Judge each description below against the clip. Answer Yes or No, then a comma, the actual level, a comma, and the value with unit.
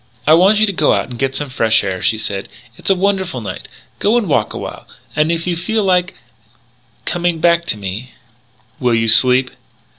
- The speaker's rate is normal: No, fast, 210 wpm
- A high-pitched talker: No, medium, 150 Hz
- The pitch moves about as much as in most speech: No, wide, 7.7 semitones